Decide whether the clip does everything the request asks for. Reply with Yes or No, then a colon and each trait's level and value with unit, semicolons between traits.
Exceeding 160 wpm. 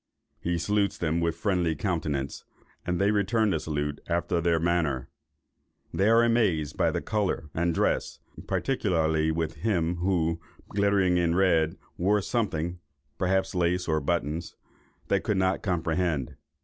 No: average, 140 wpm